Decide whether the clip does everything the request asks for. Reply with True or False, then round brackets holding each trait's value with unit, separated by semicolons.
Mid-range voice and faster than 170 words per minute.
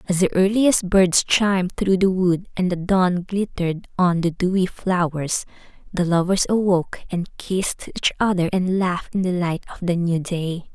True (180 Hz; 180 wpm)